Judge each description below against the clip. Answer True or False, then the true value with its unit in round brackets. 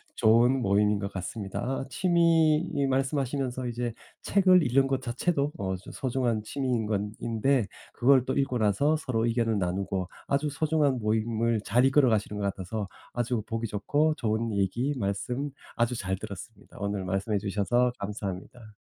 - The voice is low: True (115 Hz)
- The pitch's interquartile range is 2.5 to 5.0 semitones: True (4.5 semitones)